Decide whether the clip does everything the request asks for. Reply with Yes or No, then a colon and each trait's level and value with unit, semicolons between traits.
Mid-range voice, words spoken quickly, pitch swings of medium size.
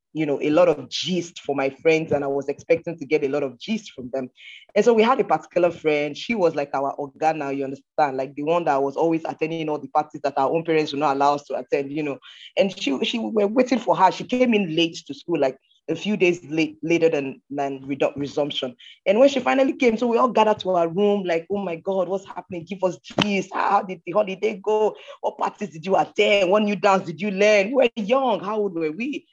No: medium, 170 Hz; fast, 250 wpm; wide, 5.9 semitones